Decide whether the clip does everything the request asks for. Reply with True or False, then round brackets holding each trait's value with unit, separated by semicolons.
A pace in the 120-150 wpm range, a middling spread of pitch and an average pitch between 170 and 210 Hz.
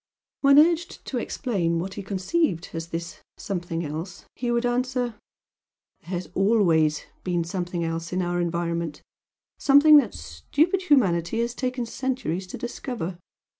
False (140 wpm; 6.8 semitones; 190 Hz)